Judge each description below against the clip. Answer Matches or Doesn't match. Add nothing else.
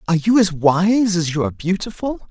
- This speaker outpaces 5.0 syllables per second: Matches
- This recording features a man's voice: Matches